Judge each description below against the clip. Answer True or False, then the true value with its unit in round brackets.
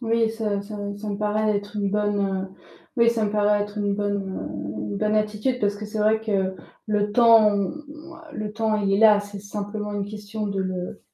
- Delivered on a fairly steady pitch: True (1.2 semitones)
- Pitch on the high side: True (210 Hz)